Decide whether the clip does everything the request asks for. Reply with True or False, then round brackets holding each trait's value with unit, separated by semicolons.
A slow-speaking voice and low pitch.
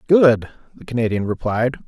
True (130 wpm; 120 Hz)